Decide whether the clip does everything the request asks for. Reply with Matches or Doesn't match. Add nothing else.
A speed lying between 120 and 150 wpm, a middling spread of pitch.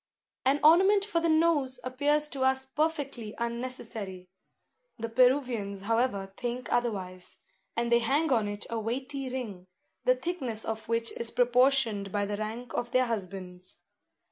Matches